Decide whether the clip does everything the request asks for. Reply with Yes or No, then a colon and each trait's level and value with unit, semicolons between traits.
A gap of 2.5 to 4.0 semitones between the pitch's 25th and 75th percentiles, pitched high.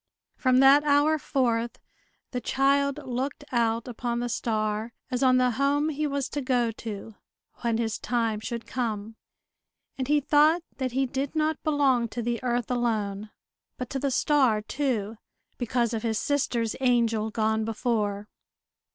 Yes: average, 3.3 semitones; high, 245 Hz